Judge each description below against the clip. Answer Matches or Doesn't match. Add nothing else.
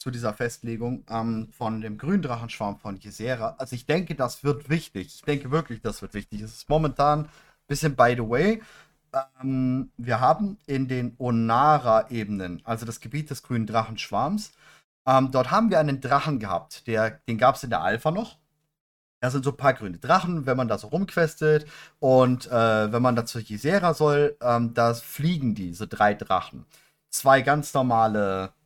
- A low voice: Matches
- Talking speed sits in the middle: Matches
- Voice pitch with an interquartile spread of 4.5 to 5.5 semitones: Matches